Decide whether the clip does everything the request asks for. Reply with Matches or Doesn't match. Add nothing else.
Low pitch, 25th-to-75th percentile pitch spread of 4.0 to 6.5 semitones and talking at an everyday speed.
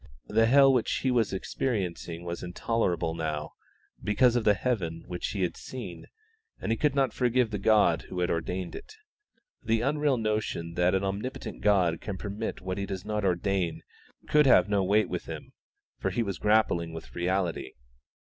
Matches